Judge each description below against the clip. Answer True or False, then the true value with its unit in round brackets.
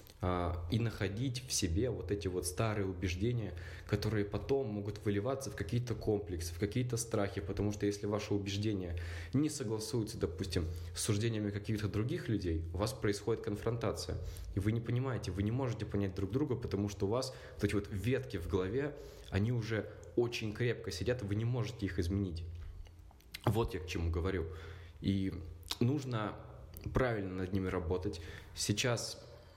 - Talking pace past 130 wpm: True (160 wpm)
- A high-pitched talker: False (100 Hz)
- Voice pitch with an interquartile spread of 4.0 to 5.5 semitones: False (3.5 semitones)